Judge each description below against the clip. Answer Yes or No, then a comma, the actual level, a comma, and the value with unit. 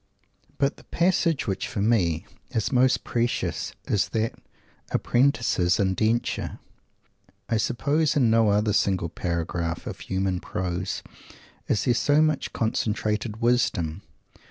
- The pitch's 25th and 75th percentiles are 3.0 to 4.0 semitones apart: No, average, 4.7 semitones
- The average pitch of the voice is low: Yes, low, 110 Hz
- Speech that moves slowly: Yes, slow, 120 wpm